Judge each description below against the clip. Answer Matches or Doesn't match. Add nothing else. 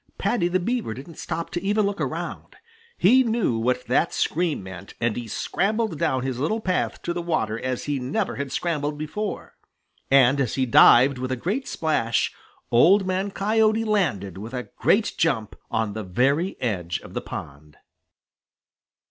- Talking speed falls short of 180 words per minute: Matches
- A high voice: Doesn't match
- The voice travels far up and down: Matches